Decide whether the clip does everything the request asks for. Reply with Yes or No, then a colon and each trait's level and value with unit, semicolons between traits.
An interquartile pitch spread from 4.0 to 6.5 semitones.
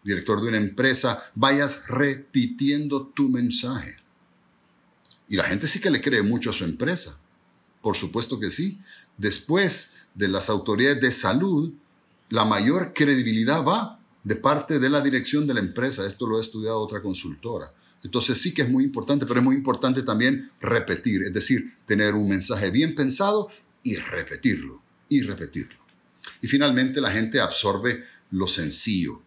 Yes: average, 4.7 semitones